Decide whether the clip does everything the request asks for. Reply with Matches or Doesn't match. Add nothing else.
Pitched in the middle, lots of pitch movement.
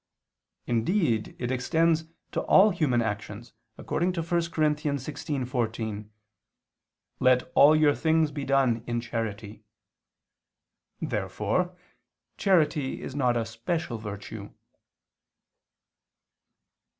Doesn't match